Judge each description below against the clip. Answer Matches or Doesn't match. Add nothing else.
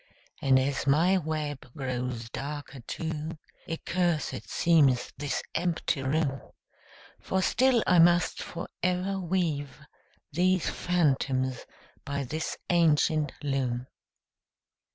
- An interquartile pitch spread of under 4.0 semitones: Doesn't match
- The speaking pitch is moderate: Matches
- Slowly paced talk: Matches